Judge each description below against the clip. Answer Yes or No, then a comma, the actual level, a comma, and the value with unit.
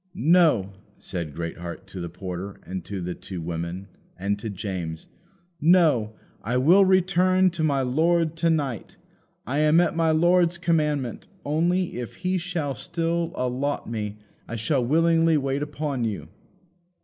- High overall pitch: No, medium, 145 Hz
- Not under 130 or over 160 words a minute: Yes, average, 150 wpm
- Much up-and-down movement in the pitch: Yes, wide, 8.6 semitones